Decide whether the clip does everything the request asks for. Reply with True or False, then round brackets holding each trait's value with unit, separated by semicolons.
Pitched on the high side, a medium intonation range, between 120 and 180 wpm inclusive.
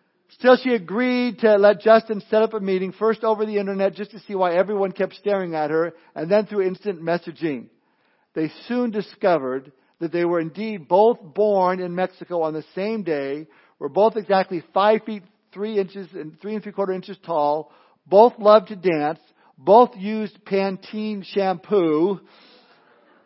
True (195 Hz; 3.6 semitones; 170 wpm)